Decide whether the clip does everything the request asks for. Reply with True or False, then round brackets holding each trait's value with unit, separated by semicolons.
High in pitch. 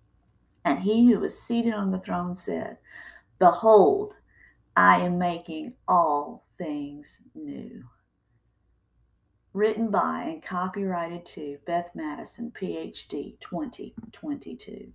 True (215 Hz)